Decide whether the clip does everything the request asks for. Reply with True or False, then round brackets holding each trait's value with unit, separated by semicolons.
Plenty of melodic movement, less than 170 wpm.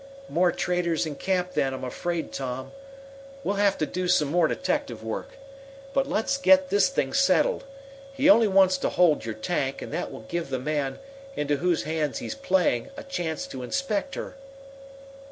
False (6.2 semitones; 175 wpm)